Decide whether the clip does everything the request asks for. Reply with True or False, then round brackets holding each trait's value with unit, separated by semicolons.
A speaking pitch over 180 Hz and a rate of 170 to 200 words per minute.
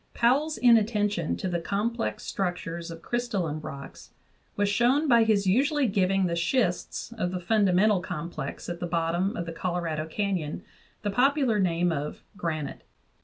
False (190 Hz; 155 wpm)